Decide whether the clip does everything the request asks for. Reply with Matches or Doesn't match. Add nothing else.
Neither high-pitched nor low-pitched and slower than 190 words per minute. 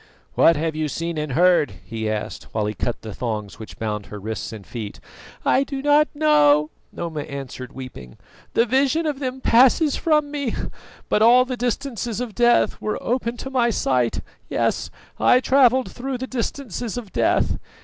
Doesn't match